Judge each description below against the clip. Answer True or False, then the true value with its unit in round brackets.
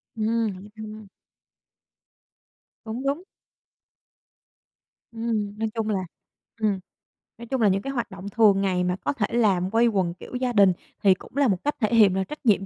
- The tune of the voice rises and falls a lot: False (3.0 semitones)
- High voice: True (215 Hz)